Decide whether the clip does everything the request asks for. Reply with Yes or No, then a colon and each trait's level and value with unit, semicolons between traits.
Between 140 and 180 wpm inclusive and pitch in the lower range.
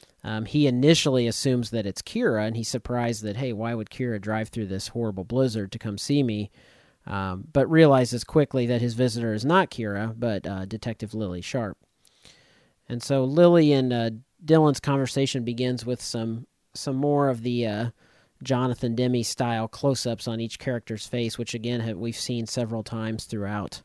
Yes: average, 175 wpm; low, 120 Hz